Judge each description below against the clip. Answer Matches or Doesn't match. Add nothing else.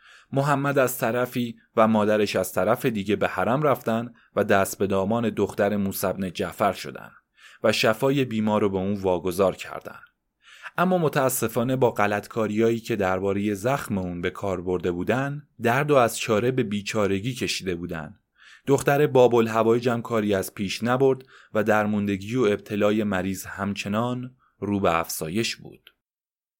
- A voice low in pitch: Matches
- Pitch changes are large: Doesn't match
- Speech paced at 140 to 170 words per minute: Matches